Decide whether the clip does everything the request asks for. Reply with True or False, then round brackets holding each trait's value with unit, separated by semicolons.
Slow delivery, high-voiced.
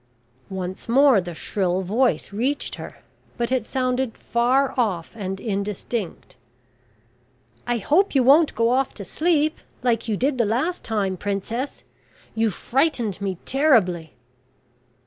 True (130 wpm; 230 Hz)